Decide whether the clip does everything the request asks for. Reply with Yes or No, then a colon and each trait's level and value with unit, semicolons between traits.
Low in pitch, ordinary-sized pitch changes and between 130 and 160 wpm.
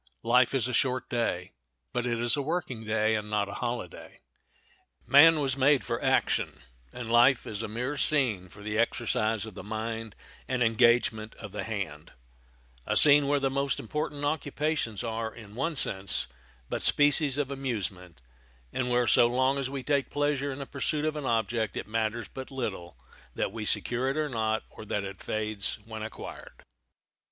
No: low, 120 Hz; average, 4.1 semitones; average, 175 wpm